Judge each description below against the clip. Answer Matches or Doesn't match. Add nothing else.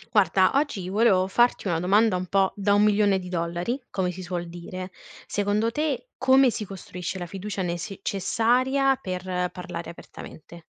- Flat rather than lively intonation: Doesn't match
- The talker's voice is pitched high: Matches